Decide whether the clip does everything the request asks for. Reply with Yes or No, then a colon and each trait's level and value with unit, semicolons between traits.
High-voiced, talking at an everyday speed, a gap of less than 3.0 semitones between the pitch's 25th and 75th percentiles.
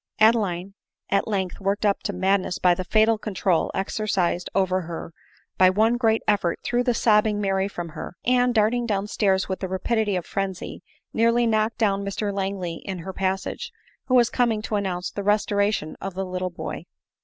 Yes: high, 200 Hz; average, 180 wpm; narrow, 2.6 semitones